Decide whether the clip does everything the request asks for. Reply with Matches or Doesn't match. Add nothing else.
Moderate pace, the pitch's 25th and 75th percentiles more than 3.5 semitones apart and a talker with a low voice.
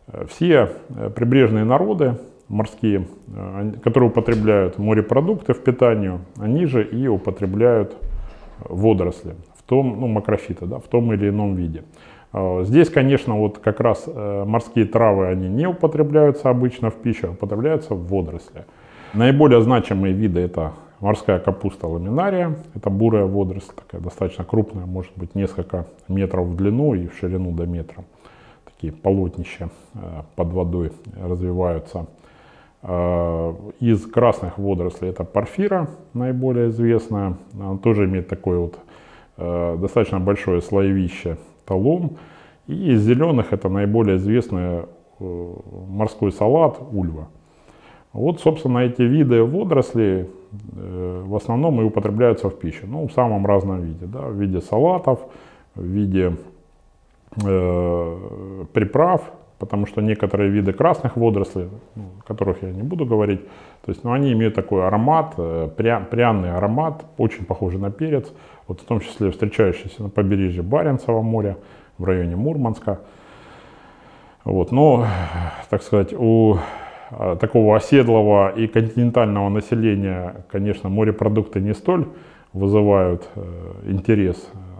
Matches